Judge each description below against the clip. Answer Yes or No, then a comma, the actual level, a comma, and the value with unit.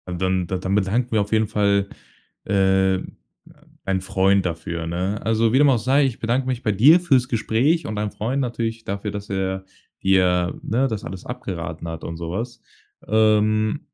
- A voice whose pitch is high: No, low, 105 Hz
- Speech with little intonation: No, average, 3.5 semitones